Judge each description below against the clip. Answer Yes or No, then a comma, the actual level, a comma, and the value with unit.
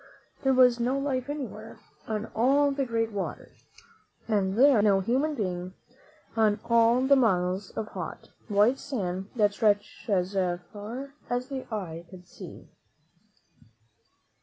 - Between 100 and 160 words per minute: Yes, average, 140 wpm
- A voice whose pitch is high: Yes, high, 220 Hz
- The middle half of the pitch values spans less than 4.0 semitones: No, average, 4.7 semitones